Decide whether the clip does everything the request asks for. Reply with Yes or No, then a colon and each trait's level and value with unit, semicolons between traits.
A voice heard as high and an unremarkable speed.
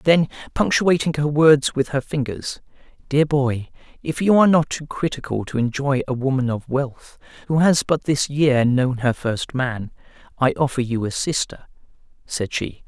No: medium, 140 Hz; average, 170 wpm